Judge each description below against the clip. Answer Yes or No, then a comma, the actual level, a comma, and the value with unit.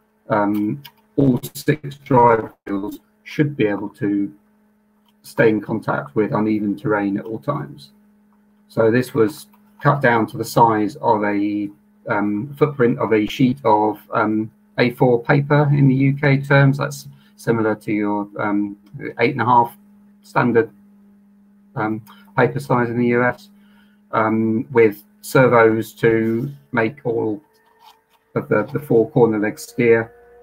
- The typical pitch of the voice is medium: No, low, 120 Hz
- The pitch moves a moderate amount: No, wide, 5.9 semitones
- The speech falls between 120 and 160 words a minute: Yes, average, 140 wpm